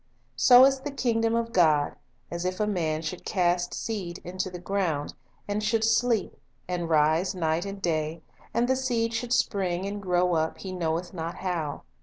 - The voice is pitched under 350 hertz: Yes, medium, 185 Hz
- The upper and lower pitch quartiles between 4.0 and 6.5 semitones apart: Yes, average, 4.8 semitones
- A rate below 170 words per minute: No, average, 180 wpm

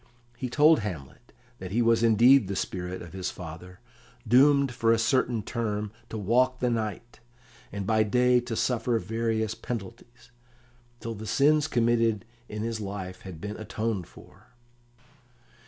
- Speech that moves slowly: No, average, 150 wpm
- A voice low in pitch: Yes, low, 115 Hz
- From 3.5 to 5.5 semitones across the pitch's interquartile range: No, average, 2.9 semitones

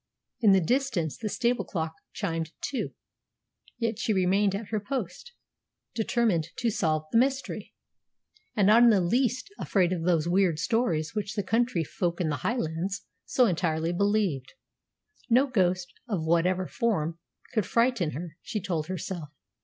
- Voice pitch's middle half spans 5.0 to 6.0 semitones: Yes, wide, 5.5 semitones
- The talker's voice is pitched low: No, high, 190 Hz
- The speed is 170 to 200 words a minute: No, average, 155 wpm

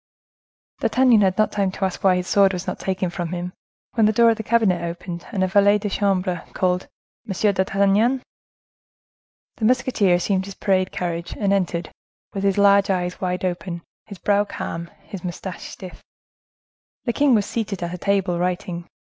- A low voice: No, high, 190 Hz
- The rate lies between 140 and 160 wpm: No, average, 185 wpm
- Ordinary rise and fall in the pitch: No, narrow, 2.2 semitones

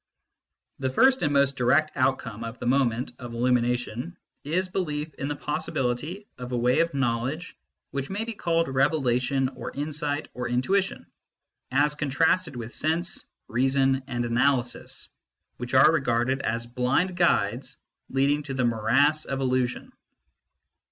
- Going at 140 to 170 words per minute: Yes, average, 145 wpm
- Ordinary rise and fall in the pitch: Yes, average, 3.7 semitones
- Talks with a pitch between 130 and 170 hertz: Yes, low, 135 Hz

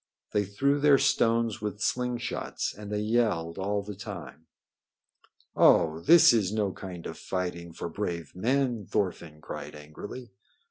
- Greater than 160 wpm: No, average, 145 wpm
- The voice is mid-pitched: No, low, 105 Hz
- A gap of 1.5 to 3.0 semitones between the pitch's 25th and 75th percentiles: No, average, 5.2 semitones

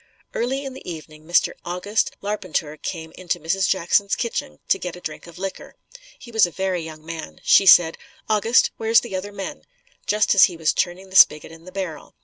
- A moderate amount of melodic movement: Yes, average, 3.8 semitones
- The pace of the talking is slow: No, average, 200 wpm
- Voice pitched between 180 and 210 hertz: Yes, medium, 185 Hz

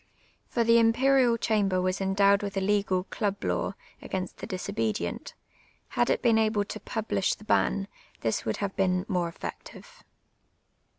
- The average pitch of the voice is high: Yes, high, 200 Hz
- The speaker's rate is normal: Yes, average, 155 wpm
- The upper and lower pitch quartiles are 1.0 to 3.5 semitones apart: Yes, average, 2.9 semitones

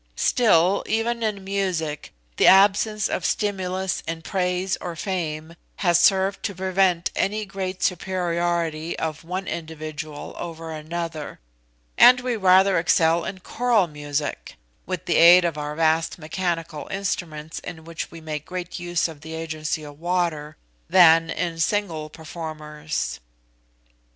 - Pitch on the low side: No, medium, 170 Hz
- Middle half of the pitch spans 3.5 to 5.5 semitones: No, average, 3.0 semitones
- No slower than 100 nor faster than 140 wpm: Yes, slow, 135 wpm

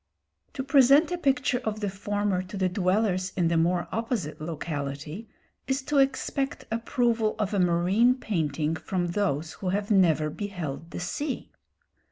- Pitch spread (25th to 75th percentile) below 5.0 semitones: No, wide, 5.5 semitones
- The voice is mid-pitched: No, high, 195 Hz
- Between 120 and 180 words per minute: Yes, average, 155 wpm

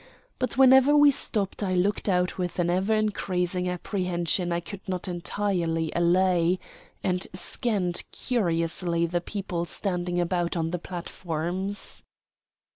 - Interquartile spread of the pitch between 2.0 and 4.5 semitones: Yes, narrow, 2.5 semitones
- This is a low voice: No, medium, 180 Hz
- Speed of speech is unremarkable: No, slow, 125 wpm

